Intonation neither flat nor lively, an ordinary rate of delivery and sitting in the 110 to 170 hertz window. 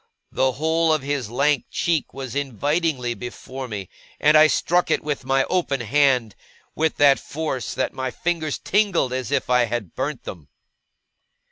Yes: average, 3.8 semitones; average, 160 wpm; low, 135 Hz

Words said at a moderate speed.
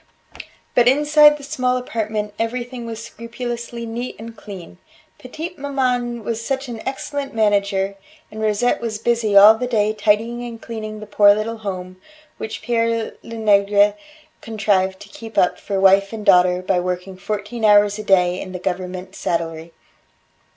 Yes: average, 155 wpm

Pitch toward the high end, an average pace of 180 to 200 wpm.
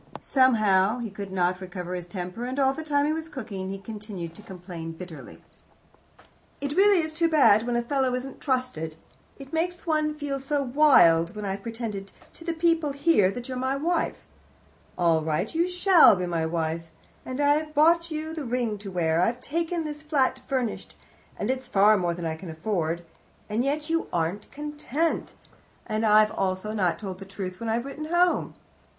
Yes: high, 235 Hz; average, 190 wpm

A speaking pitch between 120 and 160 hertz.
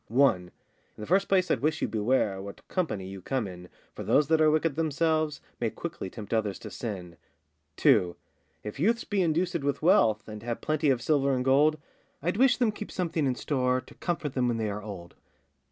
Yes: low, 135 Hz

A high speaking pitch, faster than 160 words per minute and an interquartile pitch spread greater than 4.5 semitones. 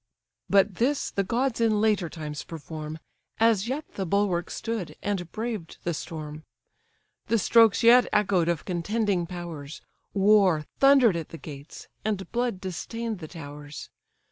No: high, 195 Hz; average, 145 wpm; wide, 5.5 semitones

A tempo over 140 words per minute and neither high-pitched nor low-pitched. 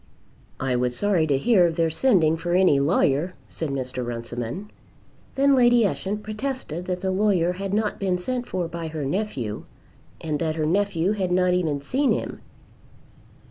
Yes: average, 170 wpm; medium, 180 Hz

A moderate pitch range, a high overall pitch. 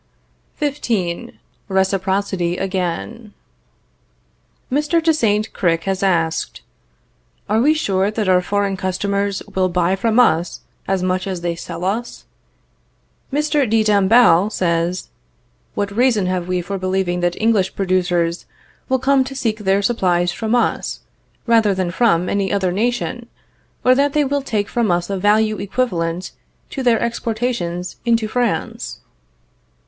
Yes: average, 4.3 semitones; high, 200 Hz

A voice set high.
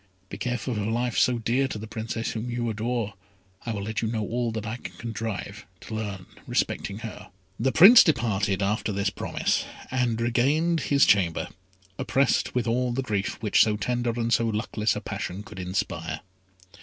No: low, 115 Hz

